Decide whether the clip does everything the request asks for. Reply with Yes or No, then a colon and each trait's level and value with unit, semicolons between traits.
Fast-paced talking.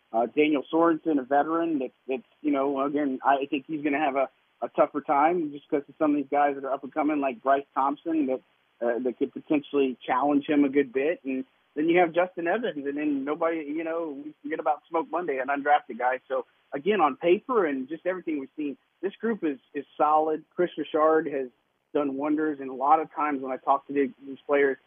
Yes: fast, 225 wpm